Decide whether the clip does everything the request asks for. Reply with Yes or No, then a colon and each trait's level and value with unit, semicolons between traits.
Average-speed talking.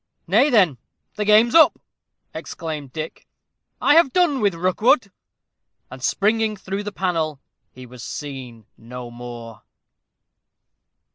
No: slow, 120 wpm